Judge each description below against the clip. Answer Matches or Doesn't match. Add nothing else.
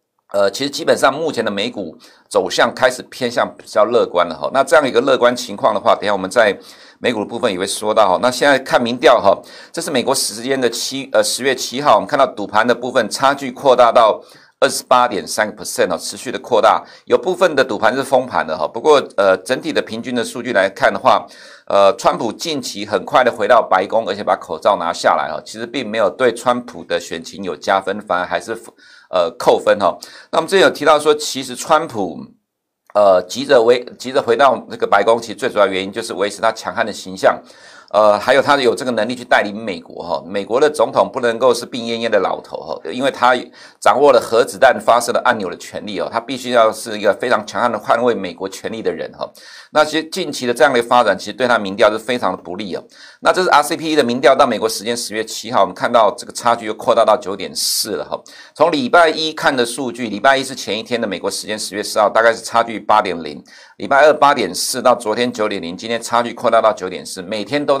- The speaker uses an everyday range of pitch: Matches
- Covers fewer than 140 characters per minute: Doesn't match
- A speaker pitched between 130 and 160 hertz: Doesn't match